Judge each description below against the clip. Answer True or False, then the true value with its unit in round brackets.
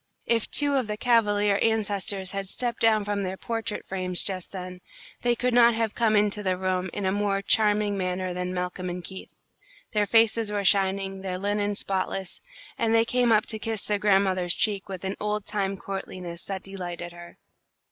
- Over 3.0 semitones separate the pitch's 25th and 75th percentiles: False (2.4 semitones)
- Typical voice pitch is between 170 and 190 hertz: False (200 Hz)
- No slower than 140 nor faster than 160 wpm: False (190 wpm)